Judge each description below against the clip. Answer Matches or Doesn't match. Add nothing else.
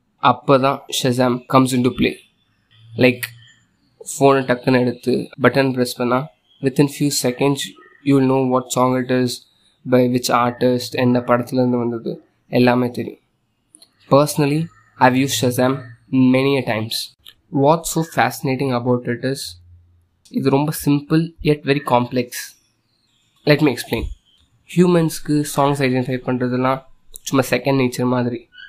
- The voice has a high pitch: Doesn't match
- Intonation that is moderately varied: Doesn't match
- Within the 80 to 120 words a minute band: Doesn't match